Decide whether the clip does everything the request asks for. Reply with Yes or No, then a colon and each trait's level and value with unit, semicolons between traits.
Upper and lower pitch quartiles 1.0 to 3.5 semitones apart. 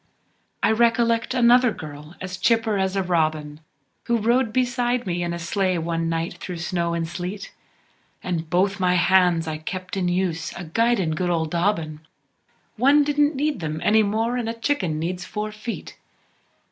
No: average, 5.3 semitones